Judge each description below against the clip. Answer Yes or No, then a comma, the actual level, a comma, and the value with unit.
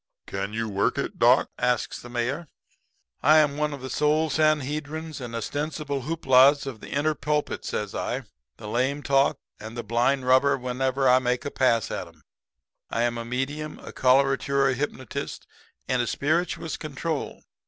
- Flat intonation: No, average, 3.3 semitones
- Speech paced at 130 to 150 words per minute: No, average, 165 wpm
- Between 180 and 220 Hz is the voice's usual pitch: No, low, 135 Hz